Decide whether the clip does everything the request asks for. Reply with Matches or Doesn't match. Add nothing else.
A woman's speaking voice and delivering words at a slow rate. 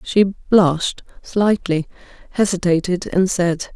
Matches